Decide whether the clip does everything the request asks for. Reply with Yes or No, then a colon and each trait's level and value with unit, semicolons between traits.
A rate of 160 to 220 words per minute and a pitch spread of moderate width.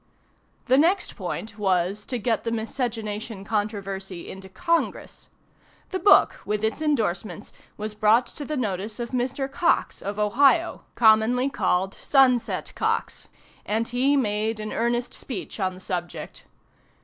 No: slow, 135 wpm; average, 3.6 semitones